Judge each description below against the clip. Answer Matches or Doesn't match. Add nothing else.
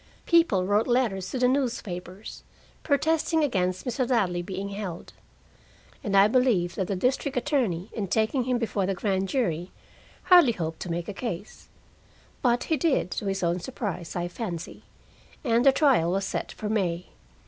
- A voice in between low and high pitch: Doesn't match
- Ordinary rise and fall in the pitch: Doesn't match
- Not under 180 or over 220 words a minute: Doesn't match